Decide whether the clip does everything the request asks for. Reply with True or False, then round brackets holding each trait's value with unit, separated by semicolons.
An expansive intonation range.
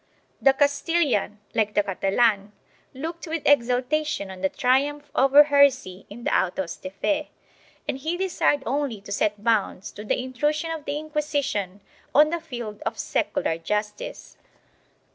True (6.1 semitones)